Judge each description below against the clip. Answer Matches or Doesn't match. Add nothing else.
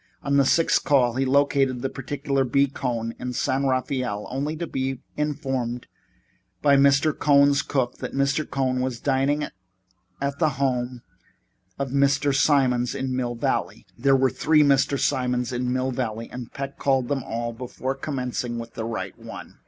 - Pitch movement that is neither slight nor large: Doesn't match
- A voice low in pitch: Matches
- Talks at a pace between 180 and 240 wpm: Doesn't match